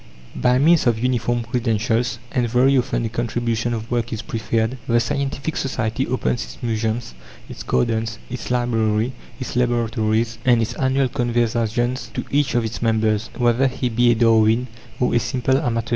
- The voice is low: Yes, low, 120 Hz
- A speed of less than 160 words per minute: No, average, 165 wpm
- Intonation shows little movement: Yes, narrow, 1.9 semitones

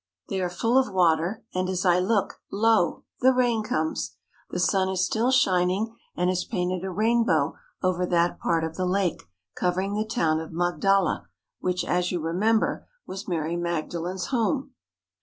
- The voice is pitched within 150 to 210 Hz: Yes, medium, 185 Hz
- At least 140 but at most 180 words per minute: Yes, average, 165 wpm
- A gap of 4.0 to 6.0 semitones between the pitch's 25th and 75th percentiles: No, average, 3.5 semitones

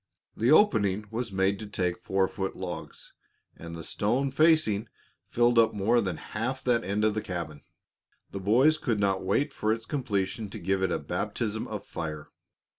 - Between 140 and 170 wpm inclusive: No, average, 180 wpm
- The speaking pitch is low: Yes, low, 105 Hz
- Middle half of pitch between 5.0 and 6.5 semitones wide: No, average, 3.8 semitones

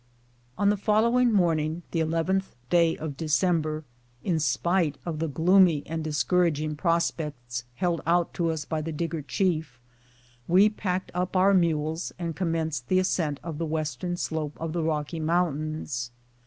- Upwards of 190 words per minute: No, average, 155 wpm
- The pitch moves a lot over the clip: No, narrow, 2.6 semitones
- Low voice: No, medium, 165 Hz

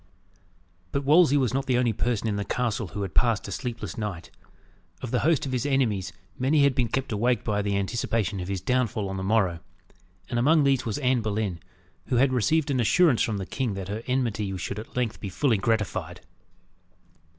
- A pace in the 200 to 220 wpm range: Yes, fast, 205 wpm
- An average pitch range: Yes, average, 4.2 semitones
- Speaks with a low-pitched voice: Yes, low, 115 Hz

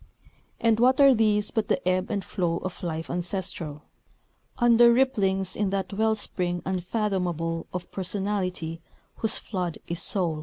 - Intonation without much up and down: No, average, 3.5 semitones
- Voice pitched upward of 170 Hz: Yes, high, 190 Hz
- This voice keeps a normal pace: Yes, average, 145 wpm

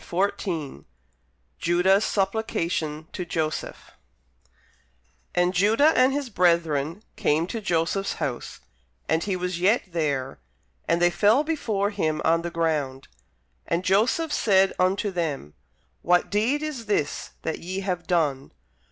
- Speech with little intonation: No, average, 4.0 semitones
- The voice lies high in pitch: No, medium, 180 Hz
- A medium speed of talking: No, slow, 125 wpm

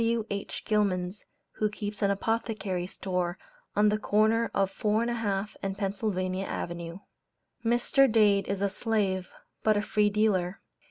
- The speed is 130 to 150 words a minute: Yes, average, 140 wpm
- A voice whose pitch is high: Yes, high, 205 Hz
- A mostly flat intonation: Yes, narrow, 2.2 semitones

